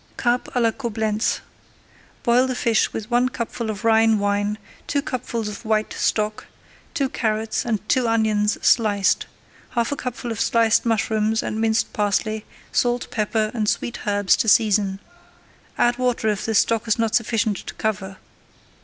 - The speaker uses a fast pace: No, average, 165 wpm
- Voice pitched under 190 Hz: No, high, 220 Hz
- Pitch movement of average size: No, narrow, 1.9 semitones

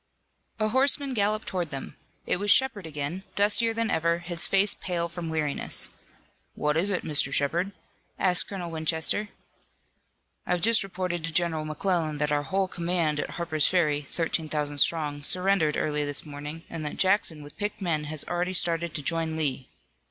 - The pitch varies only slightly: No, average, 3.8 semitones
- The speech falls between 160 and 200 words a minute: Yes, average, 170 wpm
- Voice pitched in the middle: Yes, medium, 170 Hz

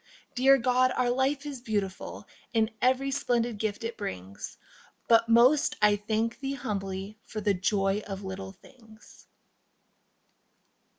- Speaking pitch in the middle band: No, high, 225 Hz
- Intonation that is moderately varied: Yes, average, 3.9 semitones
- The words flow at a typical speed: No, slow, 130 wpm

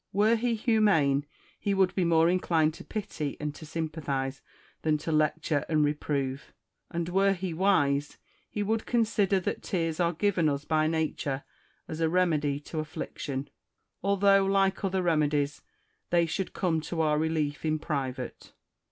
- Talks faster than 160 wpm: No, average, 155 wpm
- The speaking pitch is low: No, medium, 160 Hz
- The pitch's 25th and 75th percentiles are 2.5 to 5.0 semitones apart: Yes, average, 4.3 semitones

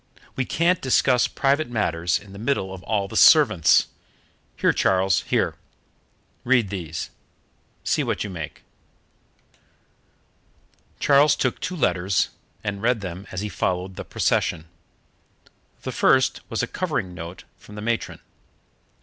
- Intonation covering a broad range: Yes, wide, 5.8 semitones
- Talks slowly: Yes, slow, 130 wpm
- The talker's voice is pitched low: Yes, low, 100 Hz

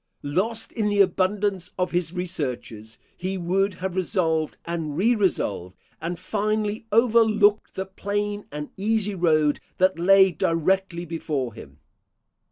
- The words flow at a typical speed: No, slow, 130 wpm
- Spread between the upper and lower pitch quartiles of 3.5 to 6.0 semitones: Yes, average, 3.9 semitones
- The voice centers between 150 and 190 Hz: Yes, medium, 185 Hz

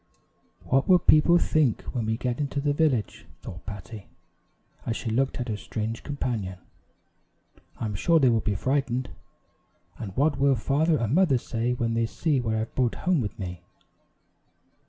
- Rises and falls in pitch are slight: No, average, 4.4 semitones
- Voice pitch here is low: Yes, low, 125 Hz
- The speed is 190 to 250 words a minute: No, average, 170 wpm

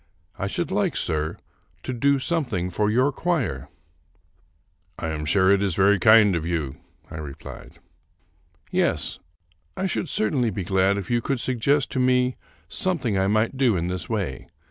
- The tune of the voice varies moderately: No, wide, 6.2 semitones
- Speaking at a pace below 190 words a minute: Yes, average, 170 wpm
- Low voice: Yes, low, 105 Hz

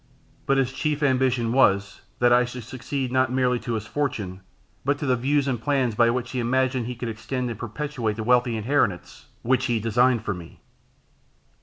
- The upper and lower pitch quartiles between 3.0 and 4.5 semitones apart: No, narrow, 2.5 semitones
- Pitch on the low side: Yes, low, 125 Hz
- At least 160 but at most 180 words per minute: No, average, 190 wpm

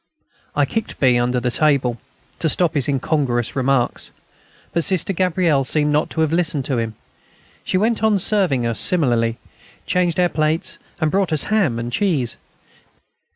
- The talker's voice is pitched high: No, medium, 155 Hz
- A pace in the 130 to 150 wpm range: No, average, 160 wpm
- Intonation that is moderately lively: No, wide, 6.3 semitones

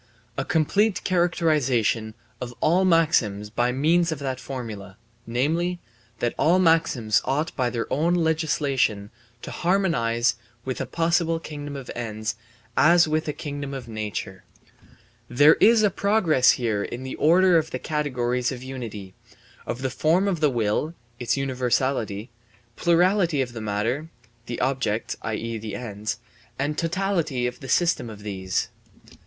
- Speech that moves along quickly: No, average, 150 wpm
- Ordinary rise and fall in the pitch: No, wide, 5.9 semitones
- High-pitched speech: No, low, 135 Hz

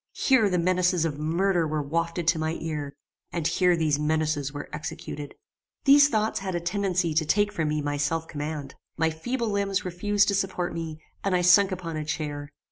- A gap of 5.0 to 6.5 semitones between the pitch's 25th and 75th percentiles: No, average, 3.7 semitones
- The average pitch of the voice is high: No, medium, 165 Hz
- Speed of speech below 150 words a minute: No, average, 195 wpm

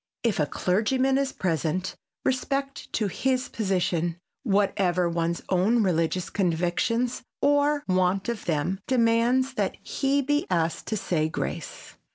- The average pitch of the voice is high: Yes, high, 200 Hz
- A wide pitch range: Yes, wide, 6.5 semitones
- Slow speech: Yes, slow, 130 wpm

